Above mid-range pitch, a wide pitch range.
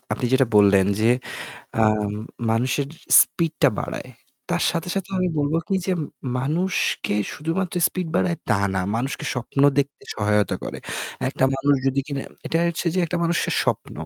No: medium, 140 Hz; wide, 6.7 semitones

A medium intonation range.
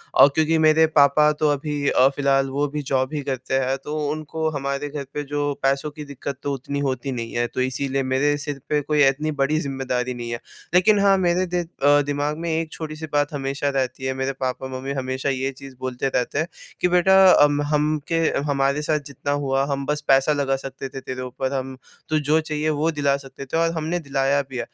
No: narrow, 2.1 semitones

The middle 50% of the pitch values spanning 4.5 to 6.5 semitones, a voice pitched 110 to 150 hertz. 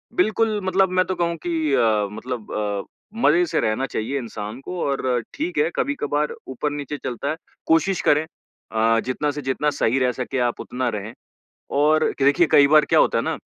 Yes: wide, 5.4 semitones; medium, 140 Hz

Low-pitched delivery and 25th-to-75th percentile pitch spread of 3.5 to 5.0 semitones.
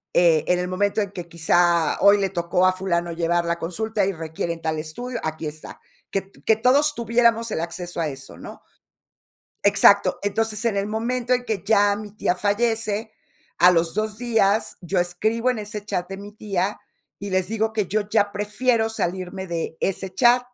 No: high, 200 Hz; average, 4.0 semitones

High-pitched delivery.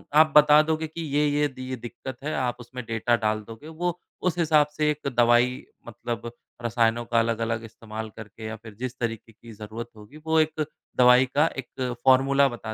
No: low, 125 Hz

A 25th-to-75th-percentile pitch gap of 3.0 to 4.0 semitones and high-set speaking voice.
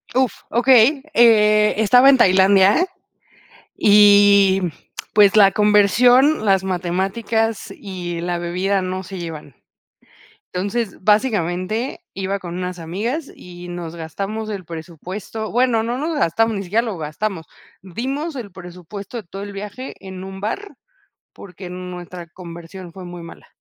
Yes: average, 3.7 semitones; high, 195 Hz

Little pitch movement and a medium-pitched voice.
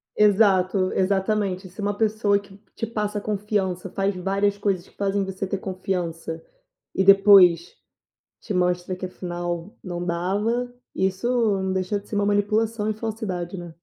No: narrow, 2.1 semitones; high, 195 Hz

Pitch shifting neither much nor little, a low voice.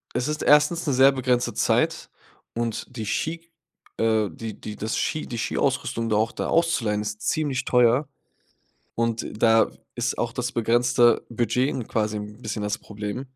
Yes: average, 3.1 semitones; low, 120 Hz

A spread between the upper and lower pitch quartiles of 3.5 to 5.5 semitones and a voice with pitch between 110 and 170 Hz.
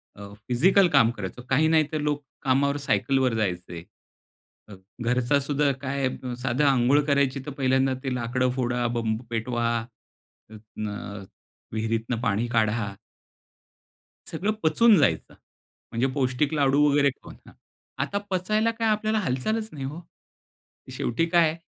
Yes: average, 4.1 semitones; low, 135 Hz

